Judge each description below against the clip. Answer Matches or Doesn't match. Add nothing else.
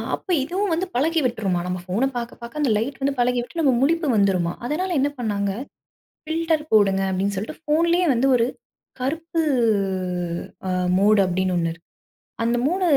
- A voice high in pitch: Matches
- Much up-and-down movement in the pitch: Matches